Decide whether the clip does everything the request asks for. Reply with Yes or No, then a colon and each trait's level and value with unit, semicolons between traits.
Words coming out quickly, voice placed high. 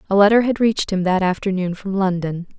Yes: fast, 210 wpm; high, 195 Hz